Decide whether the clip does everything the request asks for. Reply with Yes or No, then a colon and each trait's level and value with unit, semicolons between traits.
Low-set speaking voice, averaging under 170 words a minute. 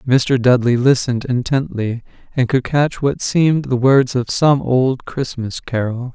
Yes: low, 130 Hz; average, 155 wpm